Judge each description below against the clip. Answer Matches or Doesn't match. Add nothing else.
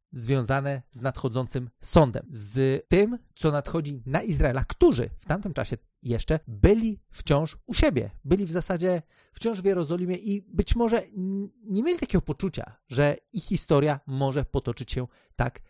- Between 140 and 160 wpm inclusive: Matches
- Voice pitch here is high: Doesn't match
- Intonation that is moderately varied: Doesn't match